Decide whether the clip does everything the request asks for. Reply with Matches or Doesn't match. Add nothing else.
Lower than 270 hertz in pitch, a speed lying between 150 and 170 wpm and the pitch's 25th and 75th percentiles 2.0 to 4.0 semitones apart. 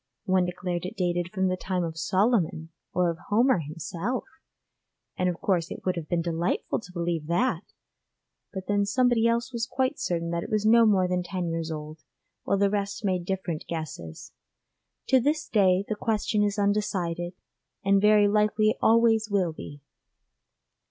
Matches